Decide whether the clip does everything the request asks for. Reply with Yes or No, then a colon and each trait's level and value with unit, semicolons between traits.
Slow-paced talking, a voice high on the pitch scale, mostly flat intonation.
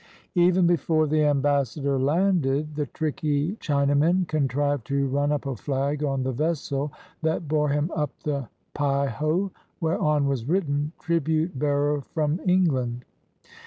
No: slow, 130 wpm; medium, 145 Hz; narrow, 2.3 semitones